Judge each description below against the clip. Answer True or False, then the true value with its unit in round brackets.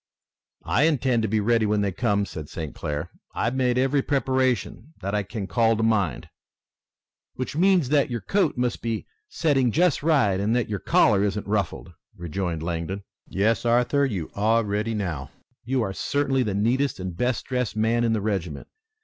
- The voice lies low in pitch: True (110 Hz)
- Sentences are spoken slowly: False (180 wpm)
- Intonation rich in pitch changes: False (4.6 semitones)